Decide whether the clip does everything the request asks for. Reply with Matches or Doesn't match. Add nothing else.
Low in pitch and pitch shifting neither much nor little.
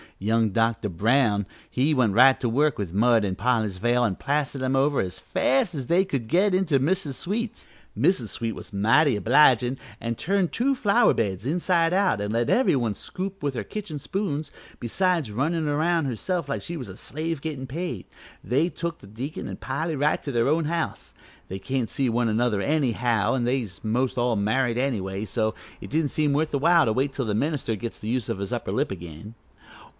Doesn't match